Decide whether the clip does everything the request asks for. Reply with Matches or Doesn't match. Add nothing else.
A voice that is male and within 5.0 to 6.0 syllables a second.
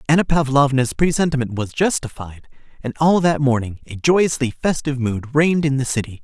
Matches